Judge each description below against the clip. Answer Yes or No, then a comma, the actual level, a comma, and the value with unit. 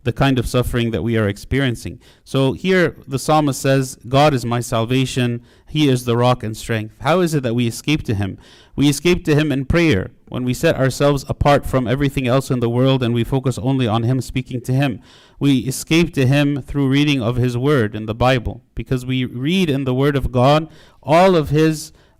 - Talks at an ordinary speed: No, fast, 215 wpm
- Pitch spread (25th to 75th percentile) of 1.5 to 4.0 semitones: Yes, average, 3.2 semitones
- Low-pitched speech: Yes, low, 130 Hz